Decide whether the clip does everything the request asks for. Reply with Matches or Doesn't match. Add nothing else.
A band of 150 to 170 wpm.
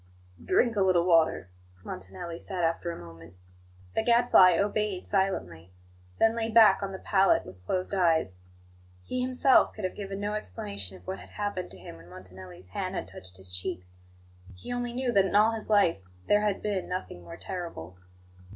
Doesn't match